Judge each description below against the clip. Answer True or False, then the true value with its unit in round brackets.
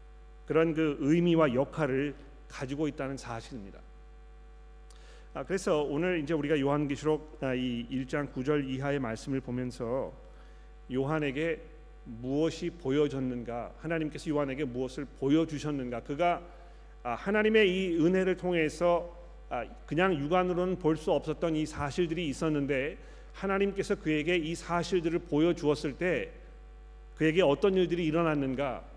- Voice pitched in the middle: True (150 Hz)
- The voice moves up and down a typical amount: True (3.8 semitones)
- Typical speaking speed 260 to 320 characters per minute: True (295 characters per minute)